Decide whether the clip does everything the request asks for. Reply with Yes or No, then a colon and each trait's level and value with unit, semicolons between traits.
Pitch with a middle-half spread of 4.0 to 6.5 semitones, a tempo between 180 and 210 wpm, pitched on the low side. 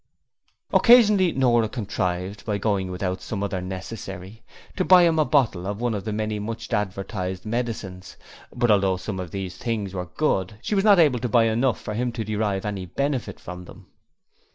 Yes: average, 4.3 semitones; average, 185 wpm; low, 105 Hz